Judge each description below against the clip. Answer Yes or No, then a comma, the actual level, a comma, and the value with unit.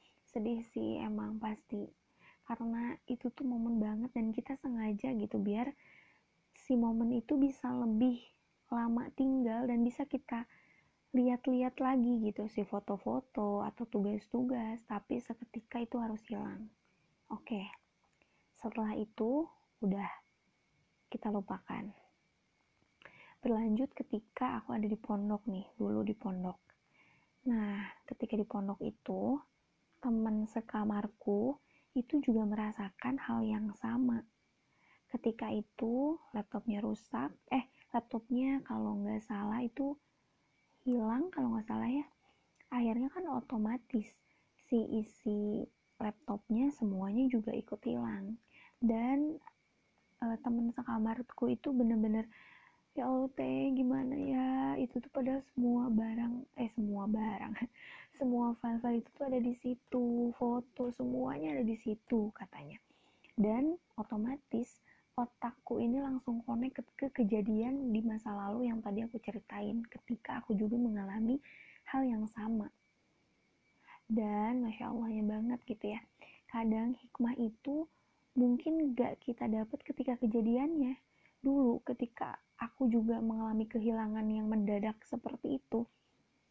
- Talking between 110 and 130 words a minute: Yes, average, 115 wpm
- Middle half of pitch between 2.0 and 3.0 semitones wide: Yes, average, 2.7 semitones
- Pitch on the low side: No, high, 235 Hz